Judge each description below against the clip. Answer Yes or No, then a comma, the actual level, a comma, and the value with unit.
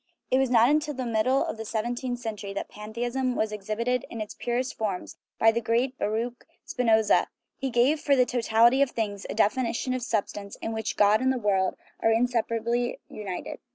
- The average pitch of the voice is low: No, high, 235 Hz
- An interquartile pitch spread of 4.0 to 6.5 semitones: No, narrow, 2.6 semitones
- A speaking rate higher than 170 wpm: Yes, average, 190 wpm